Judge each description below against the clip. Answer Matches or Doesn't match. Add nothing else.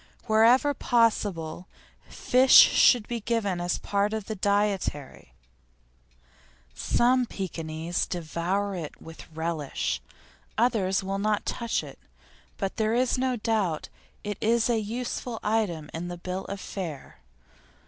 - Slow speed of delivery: Matches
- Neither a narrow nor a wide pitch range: Matches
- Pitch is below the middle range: Doesn't match